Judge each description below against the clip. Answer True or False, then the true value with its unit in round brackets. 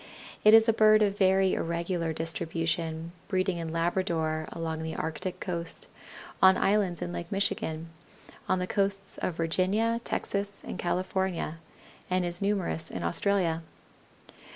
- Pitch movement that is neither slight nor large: True (3.0 semitones)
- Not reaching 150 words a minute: True (135 wpm)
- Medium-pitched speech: True (180 Hz)